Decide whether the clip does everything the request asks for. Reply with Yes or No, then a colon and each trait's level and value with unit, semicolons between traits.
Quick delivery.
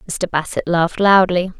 No: average, 150 wpm